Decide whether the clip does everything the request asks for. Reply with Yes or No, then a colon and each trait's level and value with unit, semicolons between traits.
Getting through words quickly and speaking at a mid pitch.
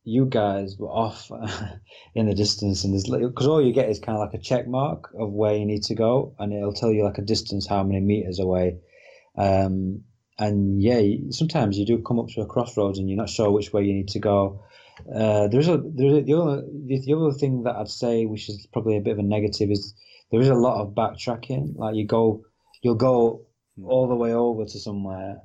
No: fast, 225 wpm; low, 110 Hz